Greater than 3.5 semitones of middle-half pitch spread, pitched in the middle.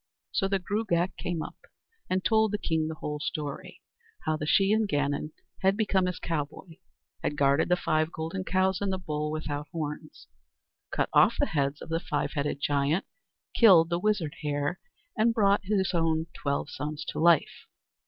Yes: average, 4.1 semitones; medium, 165 Hz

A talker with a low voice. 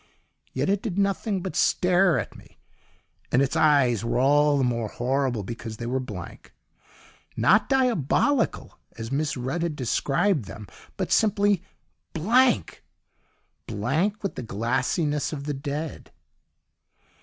No: medium, 145 Hz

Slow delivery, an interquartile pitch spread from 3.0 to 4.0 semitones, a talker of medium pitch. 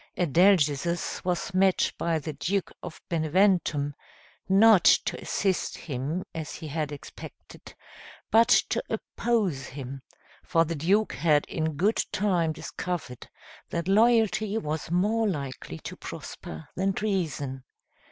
No: slow, 125 wpm; average, 4.8 semitones; medium, 170 Hz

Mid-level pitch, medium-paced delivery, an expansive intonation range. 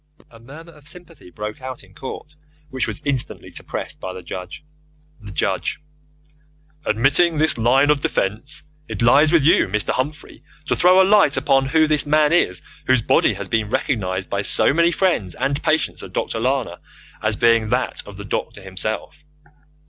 No: low, 130 Hz; average, 175 wpm; wide, 6.2 semitones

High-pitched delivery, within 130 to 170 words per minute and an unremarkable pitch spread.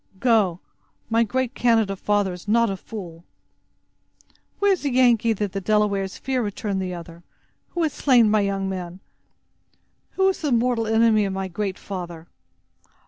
Yes: high, 210 Hz; average, 160 wpm; average, 3.5 semitones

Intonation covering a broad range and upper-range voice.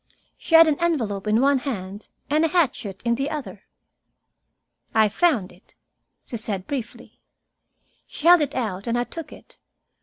Yes: wide, 6.6 semitones; high, 240 Hz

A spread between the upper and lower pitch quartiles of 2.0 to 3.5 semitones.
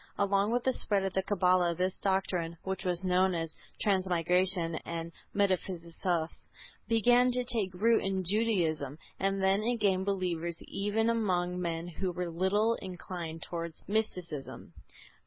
Yes: average, 2.8 semitones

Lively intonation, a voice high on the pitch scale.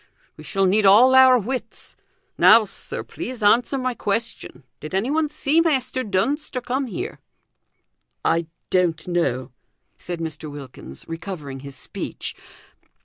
Yes: wide, 7.7 semitones; high, 205 Hz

